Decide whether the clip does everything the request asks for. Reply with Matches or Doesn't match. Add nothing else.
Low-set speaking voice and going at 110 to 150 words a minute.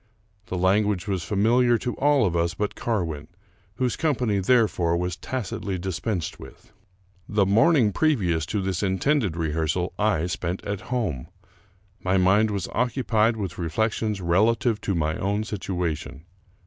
Matches